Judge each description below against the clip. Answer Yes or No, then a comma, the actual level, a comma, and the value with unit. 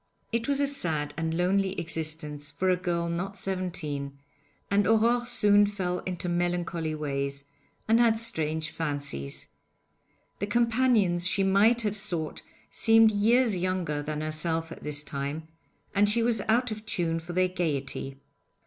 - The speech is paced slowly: No, average, 150 wpm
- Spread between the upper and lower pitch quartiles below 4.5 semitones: No, average, 5.1 semitones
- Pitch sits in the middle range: Yes, medium, 180 Hz